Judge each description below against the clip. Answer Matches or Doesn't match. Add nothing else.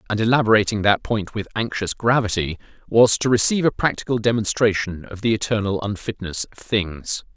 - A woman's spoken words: Doesn't match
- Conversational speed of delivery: Matches